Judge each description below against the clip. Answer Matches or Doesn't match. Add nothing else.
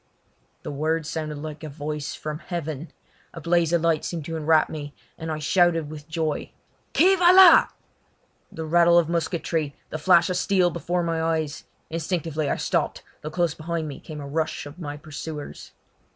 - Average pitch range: Doesn't match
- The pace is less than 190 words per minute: Matches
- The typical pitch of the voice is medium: Matches